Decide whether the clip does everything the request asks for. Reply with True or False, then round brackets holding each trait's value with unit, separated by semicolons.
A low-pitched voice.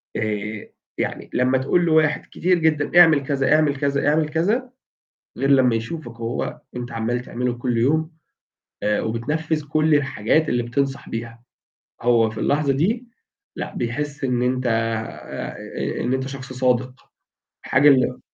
True (130 Hz)